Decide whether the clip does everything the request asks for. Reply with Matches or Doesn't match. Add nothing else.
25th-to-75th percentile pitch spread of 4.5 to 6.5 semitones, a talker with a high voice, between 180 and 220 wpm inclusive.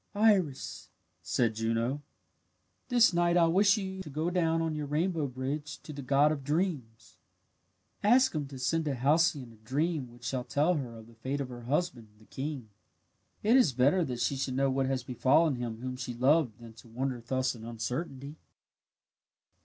Doesn't match